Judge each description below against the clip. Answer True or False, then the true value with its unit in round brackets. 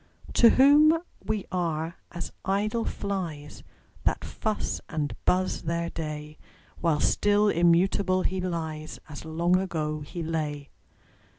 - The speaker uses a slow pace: True (120 wpm)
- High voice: False (170 Hz)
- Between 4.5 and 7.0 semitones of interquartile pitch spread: False (3.8 semitones)